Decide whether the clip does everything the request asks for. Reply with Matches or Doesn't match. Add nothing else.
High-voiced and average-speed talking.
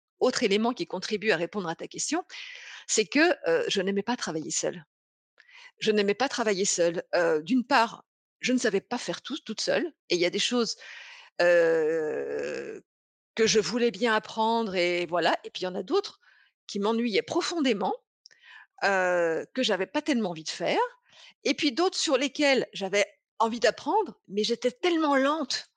Matches